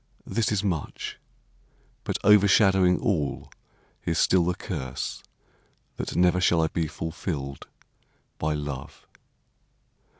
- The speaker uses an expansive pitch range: No, average, 4.2 semitones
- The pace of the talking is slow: Yes, slow, 105 wpm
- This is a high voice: No, very low, 85 Hz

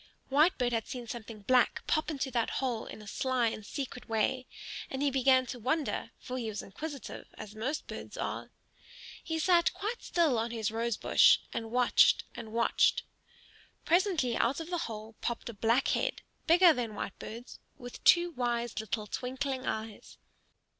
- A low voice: No, high, 245 Hz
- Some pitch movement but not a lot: Yes, average, 4.1 semitones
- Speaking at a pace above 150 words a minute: Yes, average, 165 wpm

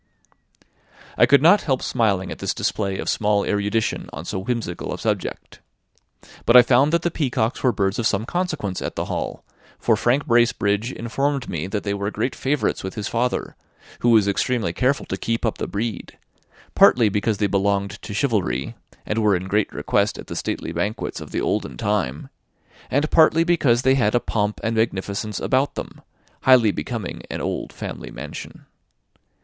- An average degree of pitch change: Yes, average, 4.0 semitones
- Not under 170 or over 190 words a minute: Yes, average, 180 wpm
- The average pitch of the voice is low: Yes, low, 110 Hz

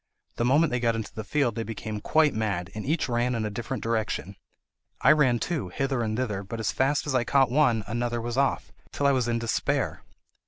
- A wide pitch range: No, average, 3.4 semitones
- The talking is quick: Yes, fast, 225 wpm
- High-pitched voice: No, low, 120 Hz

